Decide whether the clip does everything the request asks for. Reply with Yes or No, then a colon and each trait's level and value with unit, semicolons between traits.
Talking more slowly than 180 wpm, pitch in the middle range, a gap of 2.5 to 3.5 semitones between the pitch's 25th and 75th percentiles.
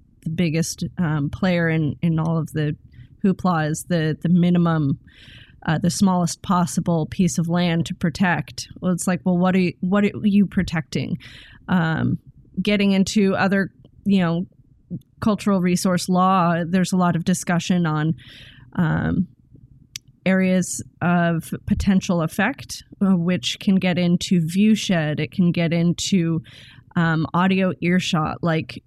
Yes: average, 140 wpm; medium, 175 Hz; average, 3.0 semitones